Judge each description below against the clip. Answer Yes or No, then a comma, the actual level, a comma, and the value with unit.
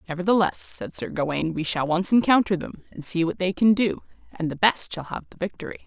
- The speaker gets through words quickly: Yes, fast, 225 wpm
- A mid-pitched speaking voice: Yes, medium, 180 Hz